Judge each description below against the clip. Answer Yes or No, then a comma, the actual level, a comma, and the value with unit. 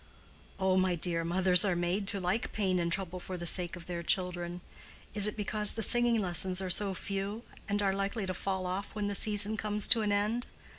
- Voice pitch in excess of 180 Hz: Yes, high, 190 Hz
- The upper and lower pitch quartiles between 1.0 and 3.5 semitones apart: Yes, narrow, 2.4 semitones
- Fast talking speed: Yes, fast, 215 wpm